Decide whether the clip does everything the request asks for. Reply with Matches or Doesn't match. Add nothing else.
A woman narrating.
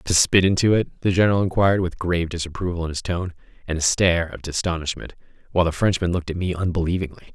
Doesn't match